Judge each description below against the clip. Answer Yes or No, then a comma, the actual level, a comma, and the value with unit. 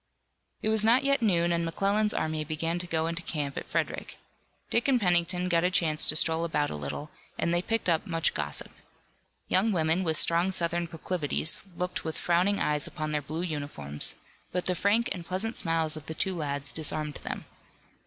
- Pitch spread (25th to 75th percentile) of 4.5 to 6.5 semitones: No, average, 2.9 semitones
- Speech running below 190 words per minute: No, average, 195 wpm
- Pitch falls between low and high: Yes, medium, 170 Hz